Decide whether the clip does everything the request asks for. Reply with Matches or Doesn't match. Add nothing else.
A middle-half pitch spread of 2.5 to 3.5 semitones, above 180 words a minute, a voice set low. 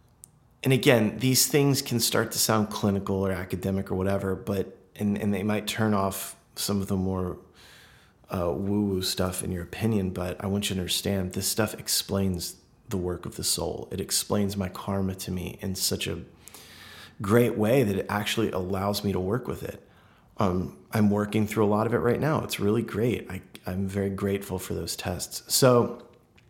Matches